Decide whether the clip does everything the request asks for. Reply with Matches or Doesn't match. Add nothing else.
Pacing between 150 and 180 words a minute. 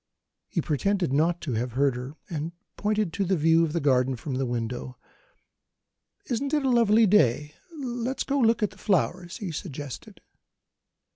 Matches